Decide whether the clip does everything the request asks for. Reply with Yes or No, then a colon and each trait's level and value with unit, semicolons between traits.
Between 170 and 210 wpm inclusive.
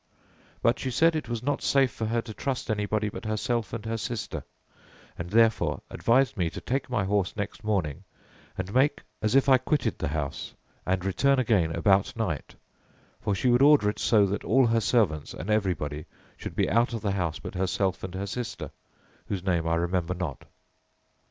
Yes: average, 190 wpm